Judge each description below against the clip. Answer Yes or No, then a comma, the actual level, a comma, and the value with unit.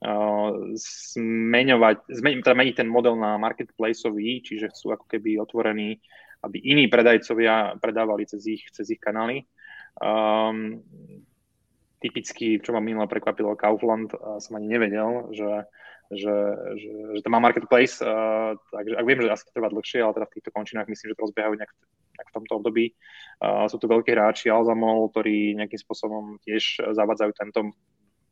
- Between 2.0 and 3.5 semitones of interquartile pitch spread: No, narrow, 1.3 semitones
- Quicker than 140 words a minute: Yes, average, 155 wpm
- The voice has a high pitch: No, low, 110 Hz